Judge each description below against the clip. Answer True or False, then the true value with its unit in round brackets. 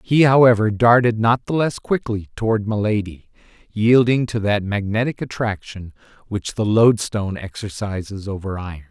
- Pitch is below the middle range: True (110 Hz)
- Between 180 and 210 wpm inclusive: False (135 wpm)